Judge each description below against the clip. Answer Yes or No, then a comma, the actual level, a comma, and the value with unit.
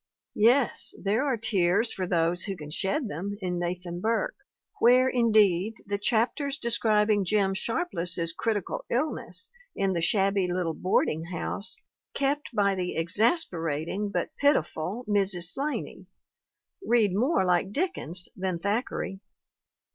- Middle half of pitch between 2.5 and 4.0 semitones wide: No, average, 4.6 semitones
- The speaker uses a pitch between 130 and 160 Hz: No, high, 200 Hz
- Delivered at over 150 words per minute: No, slow, 135 wpm